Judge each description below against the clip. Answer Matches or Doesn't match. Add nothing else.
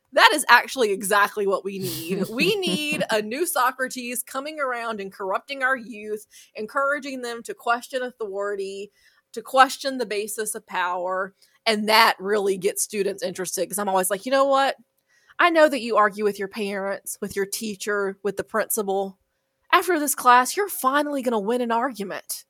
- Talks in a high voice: Matches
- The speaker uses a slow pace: Doesn't match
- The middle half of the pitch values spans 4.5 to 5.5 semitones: Matches